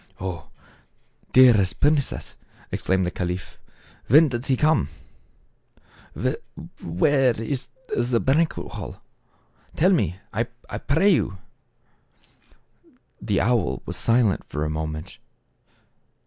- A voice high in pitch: No, low, 120 Hz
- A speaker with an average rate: No, slow, 105 wpm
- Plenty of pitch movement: Yes, wide, 6.9 semitones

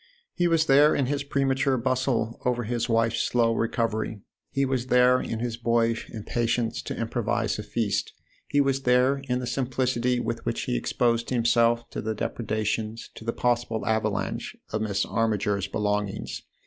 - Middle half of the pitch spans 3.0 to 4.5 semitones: No, narrow, 2.4 semitones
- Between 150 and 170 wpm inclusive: Yes, average, 165 wpm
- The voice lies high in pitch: No, low, 120 Hz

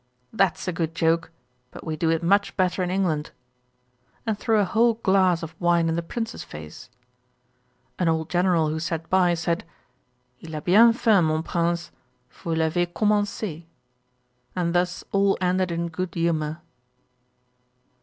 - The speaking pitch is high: No, medium, 175 Hz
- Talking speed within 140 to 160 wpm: Yes, average, 155 wpm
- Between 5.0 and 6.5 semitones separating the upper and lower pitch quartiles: No, narrow, 2.6 semitones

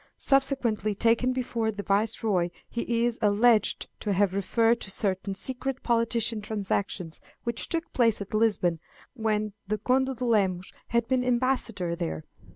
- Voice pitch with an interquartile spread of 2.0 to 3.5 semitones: Yes, average, 3.1 semitones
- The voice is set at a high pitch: Yes, high, 225 Hz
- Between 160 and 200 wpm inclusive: No, average, 145 wpm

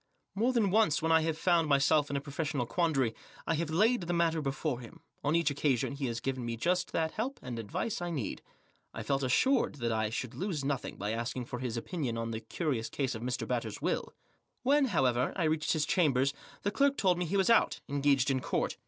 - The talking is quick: Yes, fast, 225 wpm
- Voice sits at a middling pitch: Yes, medium, 145 Hz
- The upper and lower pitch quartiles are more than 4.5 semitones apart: Yes, wide, 5.5 semitones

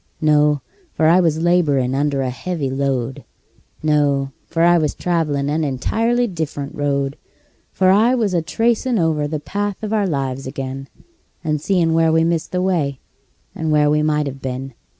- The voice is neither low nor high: Yes, medium, 155 Hz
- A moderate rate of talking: Yes, average, 170 wpm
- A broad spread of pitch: No, average, 4.0 semitones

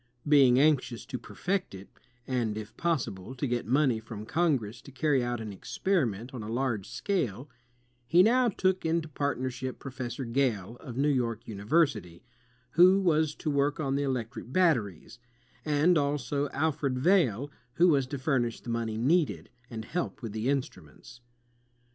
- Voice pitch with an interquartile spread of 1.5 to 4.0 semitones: No, average, 4.8 semitones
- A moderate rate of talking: Yes, average, 155 wpm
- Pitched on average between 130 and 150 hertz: Yes, low, 135 Hz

